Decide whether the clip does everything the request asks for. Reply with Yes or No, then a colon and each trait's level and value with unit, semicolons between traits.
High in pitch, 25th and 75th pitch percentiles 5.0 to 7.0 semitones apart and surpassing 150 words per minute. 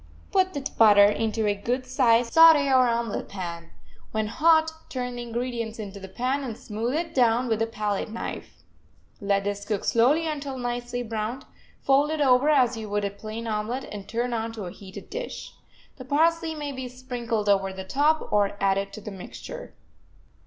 No: high, 235 Hz; average, 4.2 semitones; average, 180 wpm